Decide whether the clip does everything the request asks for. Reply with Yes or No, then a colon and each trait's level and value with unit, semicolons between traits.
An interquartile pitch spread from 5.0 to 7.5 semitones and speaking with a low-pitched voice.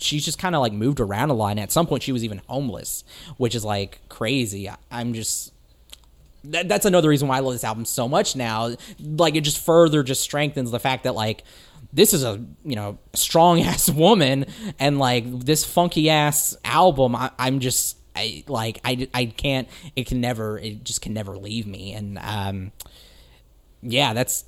Yes: wide, 5.4 semitones; low, 125 Hz